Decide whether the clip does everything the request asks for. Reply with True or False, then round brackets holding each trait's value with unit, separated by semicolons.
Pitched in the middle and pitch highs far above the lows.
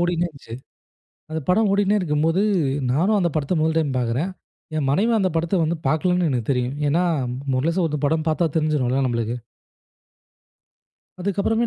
False (160 Hz; 4.4 semitones)